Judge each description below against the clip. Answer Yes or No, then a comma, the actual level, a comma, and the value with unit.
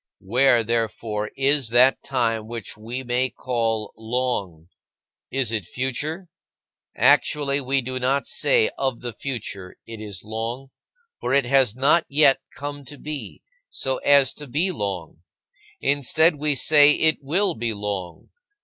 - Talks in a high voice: No, low, 130 Hz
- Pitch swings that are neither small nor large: Yes, average, 3.9 semitones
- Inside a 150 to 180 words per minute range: No, average, 140 wpm